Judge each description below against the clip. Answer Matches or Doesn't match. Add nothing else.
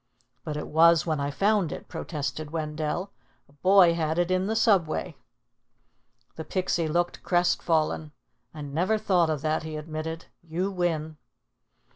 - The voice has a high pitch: Doesn't match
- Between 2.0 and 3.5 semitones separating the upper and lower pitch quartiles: Matches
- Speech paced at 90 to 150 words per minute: Matches